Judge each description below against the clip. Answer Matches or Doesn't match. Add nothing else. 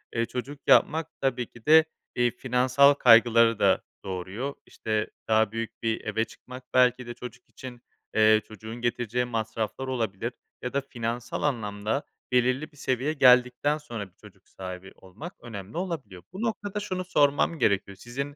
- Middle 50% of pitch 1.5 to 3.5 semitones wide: Doesn't match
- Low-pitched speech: Matches